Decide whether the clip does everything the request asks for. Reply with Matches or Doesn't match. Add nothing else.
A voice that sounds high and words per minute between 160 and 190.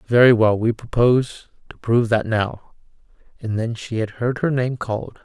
Doesn't match